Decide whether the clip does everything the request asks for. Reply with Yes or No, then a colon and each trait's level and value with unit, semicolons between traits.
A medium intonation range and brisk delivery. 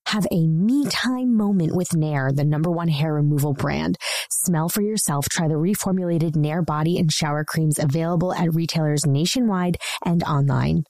No: average, 3.2 semitones; average, 165 wpm